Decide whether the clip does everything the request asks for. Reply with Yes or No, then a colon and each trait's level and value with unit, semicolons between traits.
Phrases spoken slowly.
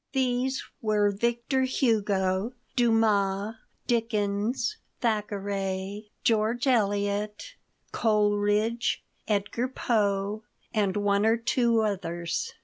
Yes: slow, 80 wpm